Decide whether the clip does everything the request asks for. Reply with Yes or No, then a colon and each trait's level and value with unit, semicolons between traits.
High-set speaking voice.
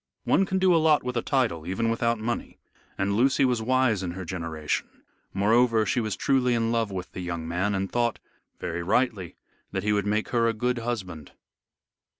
No: low, 110 Hz